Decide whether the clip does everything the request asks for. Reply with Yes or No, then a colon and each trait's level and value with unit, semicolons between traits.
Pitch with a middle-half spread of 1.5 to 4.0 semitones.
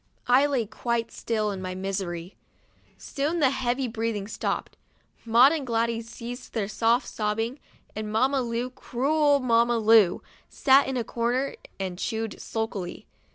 Yes: average, 3.0 semitones